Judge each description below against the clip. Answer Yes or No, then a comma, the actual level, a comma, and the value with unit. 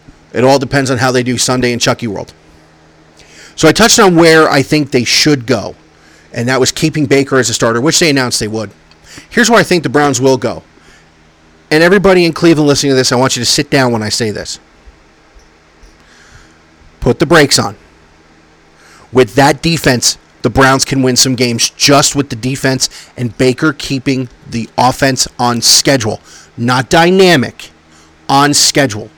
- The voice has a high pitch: No, low, 125 Hz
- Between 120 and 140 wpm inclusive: No, average, 180 wpm